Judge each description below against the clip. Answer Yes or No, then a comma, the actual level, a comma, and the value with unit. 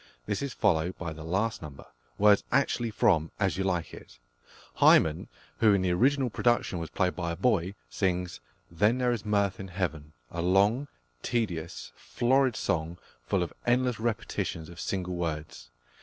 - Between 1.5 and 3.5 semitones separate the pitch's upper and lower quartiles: No, average, 4.9 semitones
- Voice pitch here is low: Yes, very low, 95 Hz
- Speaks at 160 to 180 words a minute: Yes, average, 165 wpm